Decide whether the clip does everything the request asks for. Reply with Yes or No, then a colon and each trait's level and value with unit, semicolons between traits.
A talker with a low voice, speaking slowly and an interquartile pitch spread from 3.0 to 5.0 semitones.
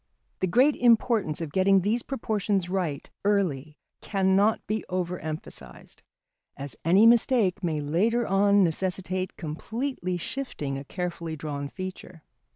No: medium, 185 Hz; slow, 125 wpm; average, 4.6 semitones